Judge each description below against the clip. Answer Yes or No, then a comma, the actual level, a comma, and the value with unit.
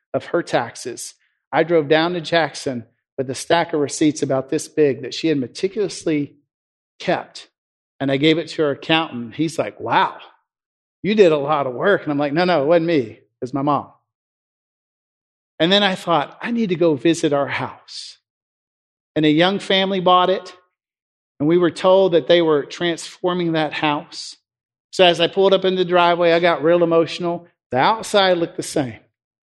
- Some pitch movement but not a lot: Yes, average, 3.3 semitones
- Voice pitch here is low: No, medium, 165 Hz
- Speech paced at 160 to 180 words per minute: No, average, 190 wpm